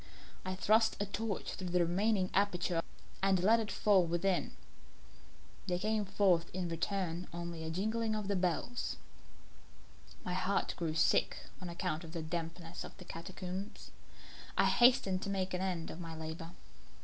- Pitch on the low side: No, medium, 185 Hz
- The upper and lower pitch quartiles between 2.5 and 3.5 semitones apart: Yes, average, 2.8 semitones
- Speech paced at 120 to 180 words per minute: Yes, average, 160 wpm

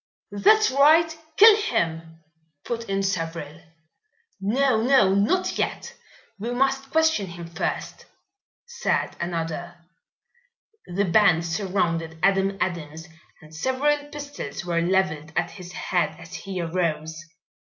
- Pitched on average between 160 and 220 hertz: Yes, high, 190 Hz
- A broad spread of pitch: Yes, wide, 7.8 semitones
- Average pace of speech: No, slow, 115 wpm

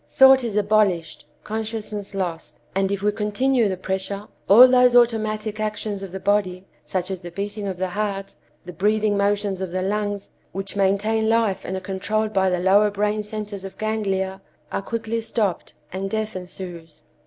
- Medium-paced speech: Yes, average, 175 wpm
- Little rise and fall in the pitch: Yes, narrow, 2.1 semitones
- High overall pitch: Yes, high, 205 Hz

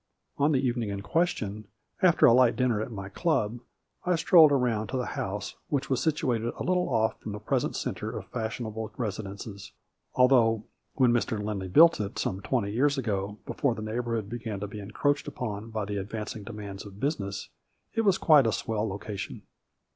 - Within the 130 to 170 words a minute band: No, average, 185 wpm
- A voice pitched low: Yes, low, 110 Hz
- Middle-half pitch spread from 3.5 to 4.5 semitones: Yes, average, 4.0 semitones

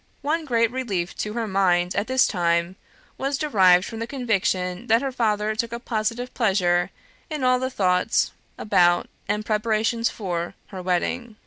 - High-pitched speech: Yes, high, 215 Hz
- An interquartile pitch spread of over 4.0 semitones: Yes, average, 4.9 semitones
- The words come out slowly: No, average, 160 wpm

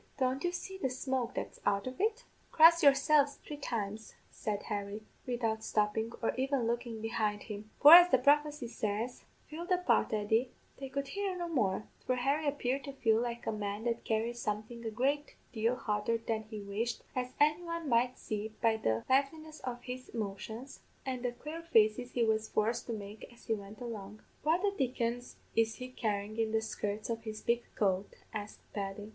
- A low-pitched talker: No, high, 235 Hz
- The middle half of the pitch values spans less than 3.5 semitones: No, average, 4.1 semitones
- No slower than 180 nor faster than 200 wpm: Yes, average, 190 wpm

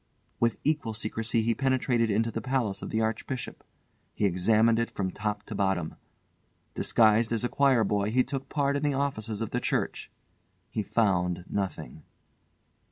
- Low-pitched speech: Yes, low, 115 Hz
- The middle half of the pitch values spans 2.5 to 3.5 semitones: Yes, average, 3.1 semitones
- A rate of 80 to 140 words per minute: No, average, 165 wpm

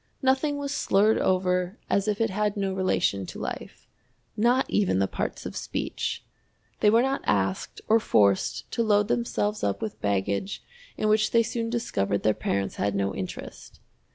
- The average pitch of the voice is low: No, high, 205 Hz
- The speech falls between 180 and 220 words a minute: No, average, 170 wpm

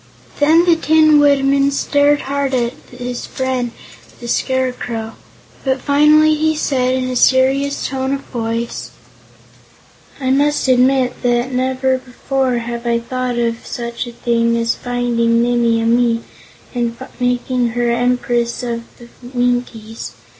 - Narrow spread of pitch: Yes, narrow, 2.2 semitones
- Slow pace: Yes, slow, 130 wpm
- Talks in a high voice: Yes, very high, 250 Hz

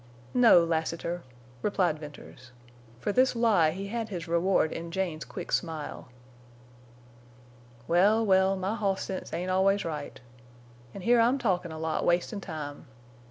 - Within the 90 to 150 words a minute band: Yes, average, 140 wpm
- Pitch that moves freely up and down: No, average, 3.6 semitones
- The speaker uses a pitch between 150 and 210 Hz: Yes, medium, 185 Hz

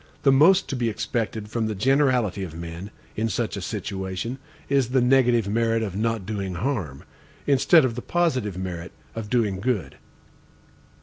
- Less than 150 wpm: No, average, 165 wpm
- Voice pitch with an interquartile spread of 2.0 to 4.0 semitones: No, average, 4.9 semitones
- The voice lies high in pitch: No, low, 115 Hz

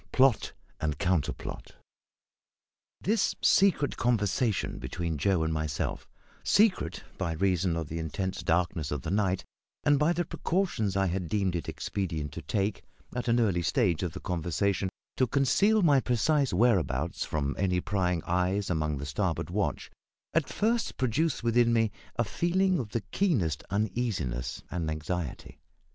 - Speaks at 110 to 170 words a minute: Yes, average, 150 wpm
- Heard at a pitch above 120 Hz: No, very low, 95 Hz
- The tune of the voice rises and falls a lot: Yes, wide, 7.0 semitones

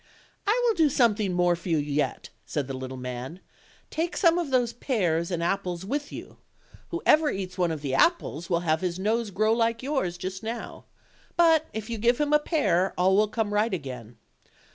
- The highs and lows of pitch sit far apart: Yes, wide, 7.1 semitones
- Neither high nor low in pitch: No, high, 200 Hz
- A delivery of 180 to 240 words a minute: Yes, average, 195 wpm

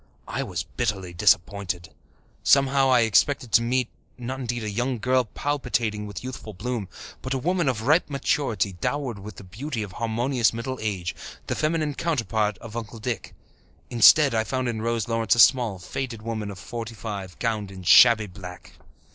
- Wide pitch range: No, average, 3.7 semitones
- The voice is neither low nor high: No, low, 115 Hz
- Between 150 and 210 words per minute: Yes, average, 175 wpm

